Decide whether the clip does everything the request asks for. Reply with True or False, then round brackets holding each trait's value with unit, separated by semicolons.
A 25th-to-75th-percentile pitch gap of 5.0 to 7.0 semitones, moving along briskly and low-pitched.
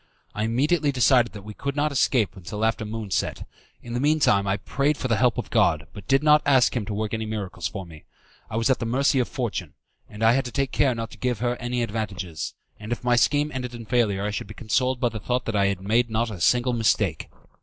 False (3.3 semitones; 260 wpm; 115 Hz)